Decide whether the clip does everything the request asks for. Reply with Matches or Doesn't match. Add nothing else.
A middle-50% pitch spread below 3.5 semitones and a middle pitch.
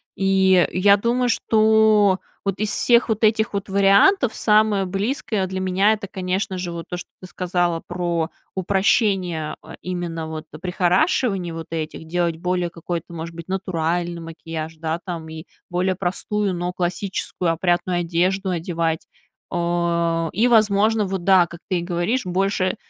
Matches